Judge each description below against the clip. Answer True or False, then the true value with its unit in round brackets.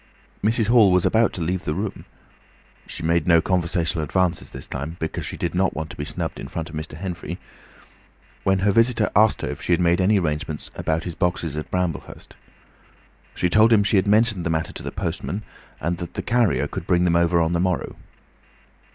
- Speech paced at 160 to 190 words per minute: False (205 wpm)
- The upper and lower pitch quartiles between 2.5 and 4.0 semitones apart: True (3.1 semitones)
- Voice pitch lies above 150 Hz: False (90 Hz)